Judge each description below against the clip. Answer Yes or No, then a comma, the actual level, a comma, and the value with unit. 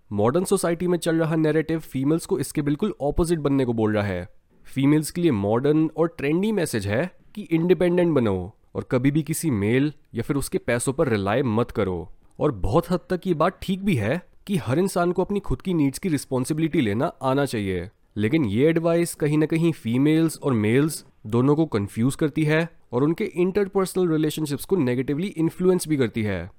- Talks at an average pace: No, fast, 195 wpm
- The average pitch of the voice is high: No, medium, 155 Hz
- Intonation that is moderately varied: No, wide, 5.7 semitones